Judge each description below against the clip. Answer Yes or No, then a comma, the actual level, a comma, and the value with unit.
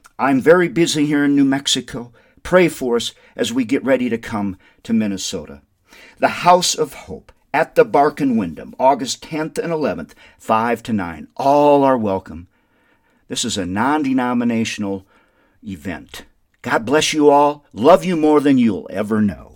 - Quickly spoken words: No, average, 165 wpm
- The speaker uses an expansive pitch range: Yes, wide, 6.8 semitones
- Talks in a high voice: No, low, 135 Hz